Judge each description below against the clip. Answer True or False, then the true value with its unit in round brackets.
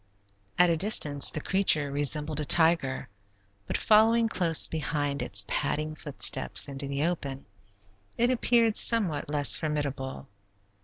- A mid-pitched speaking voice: True (155 Hz)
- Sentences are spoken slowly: True (125 wpm)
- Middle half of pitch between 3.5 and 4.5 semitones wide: True (4.0 semitones)